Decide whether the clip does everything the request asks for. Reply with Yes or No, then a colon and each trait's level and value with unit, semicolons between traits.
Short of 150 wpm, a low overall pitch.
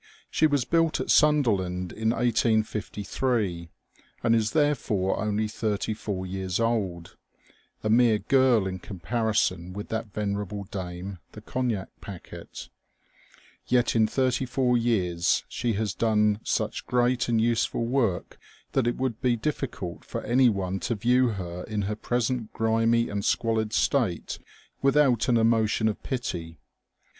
Yes: average, 140 wpm; low, 110 Hz